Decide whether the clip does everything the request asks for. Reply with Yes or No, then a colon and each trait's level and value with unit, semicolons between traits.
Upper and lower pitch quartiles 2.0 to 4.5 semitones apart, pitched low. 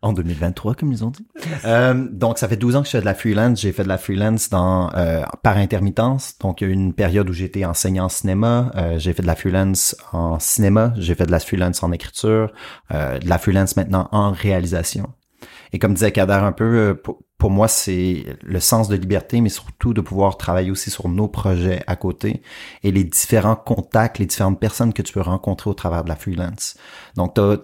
Yes: average, 3.3 semitones; low, 100 Hz